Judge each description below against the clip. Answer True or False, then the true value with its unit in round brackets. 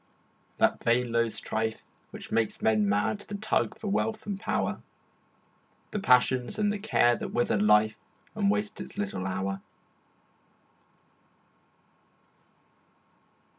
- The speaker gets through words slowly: True (120 wpm)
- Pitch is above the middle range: False (120 Hz)